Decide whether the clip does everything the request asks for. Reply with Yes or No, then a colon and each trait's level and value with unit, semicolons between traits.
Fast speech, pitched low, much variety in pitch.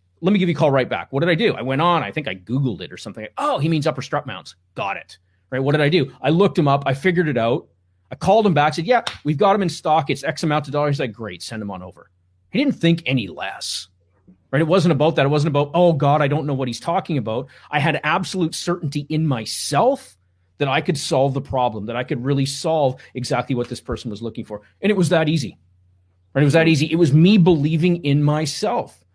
No: fast, 265 wpm; medium, 145 Hz; wide, 6.0 semitones